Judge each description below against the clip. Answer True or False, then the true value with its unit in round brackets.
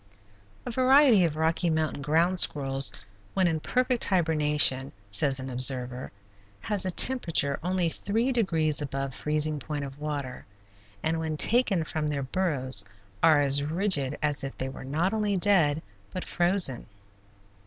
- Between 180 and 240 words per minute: False (145 wpm)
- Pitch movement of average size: True (5.0 semitones)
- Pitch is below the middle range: False (155 Hz)